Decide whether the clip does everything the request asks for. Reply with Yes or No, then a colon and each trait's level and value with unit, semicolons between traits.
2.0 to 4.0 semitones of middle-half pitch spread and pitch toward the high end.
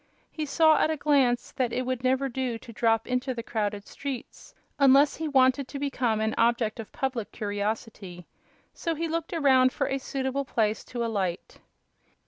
Yes: average, 3.6 semitones; very high, 255 Hz